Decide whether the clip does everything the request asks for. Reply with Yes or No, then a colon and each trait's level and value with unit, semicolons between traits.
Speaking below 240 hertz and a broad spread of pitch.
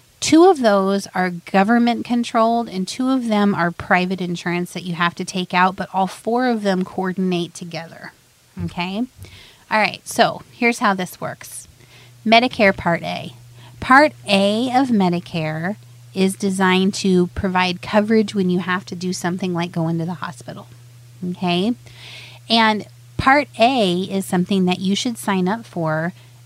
No: medium, 185 Hz; average, 3.3 semitones